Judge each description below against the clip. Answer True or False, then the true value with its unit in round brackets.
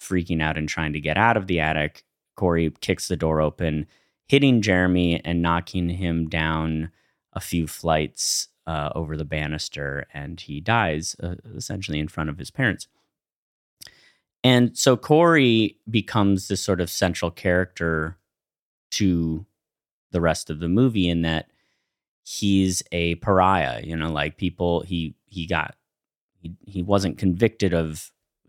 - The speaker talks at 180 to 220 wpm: False (145 wpm)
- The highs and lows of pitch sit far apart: False (3.6 semitones)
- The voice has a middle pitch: False (85 Hz)